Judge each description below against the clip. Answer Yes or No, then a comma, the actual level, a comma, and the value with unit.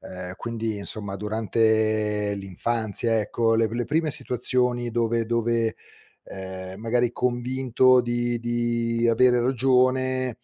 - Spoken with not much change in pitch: Yes, narrow, 2.0 semitones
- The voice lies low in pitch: Yes, low, 115 Hz